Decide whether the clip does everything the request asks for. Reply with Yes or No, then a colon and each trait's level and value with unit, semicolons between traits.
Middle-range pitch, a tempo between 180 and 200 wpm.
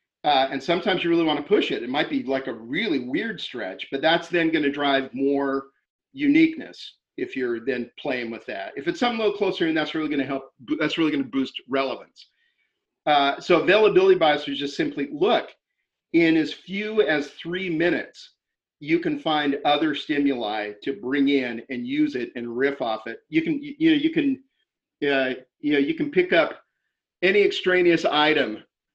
Yes: medium, 155 Hz; average, 195 wpm